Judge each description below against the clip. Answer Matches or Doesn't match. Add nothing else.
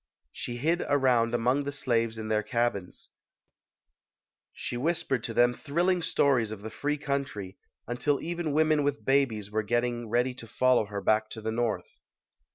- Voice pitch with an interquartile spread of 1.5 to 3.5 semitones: Doesn't match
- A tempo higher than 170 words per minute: Doesn't match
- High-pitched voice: Doesn't match